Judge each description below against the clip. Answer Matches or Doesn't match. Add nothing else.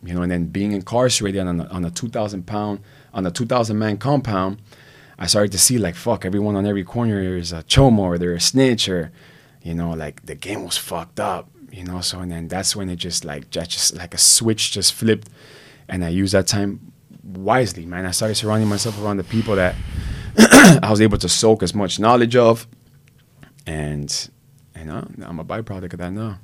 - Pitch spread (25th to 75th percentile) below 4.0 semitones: Doesn't match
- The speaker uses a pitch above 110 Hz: Doesn't match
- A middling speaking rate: Doesn't match